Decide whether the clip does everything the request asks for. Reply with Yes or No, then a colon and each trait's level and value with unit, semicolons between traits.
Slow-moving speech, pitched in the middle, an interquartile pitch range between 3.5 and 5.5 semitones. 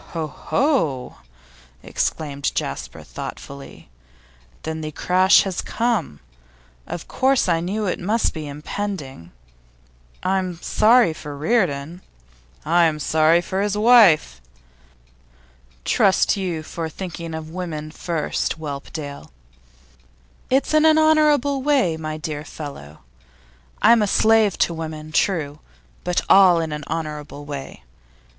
Yes: slow, 115 wpm; medium, 165 Hz; average, 5.2 semitones